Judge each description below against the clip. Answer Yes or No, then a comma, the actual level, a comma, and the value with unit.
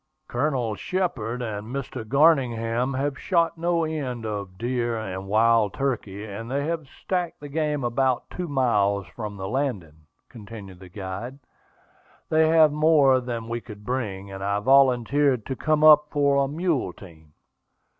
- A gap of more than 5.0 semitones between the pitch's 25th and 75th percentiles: Yes, wide, 5.6 semitones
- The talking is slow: No, average, 155 wpm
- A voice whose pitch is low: Yes, low, 125 Hz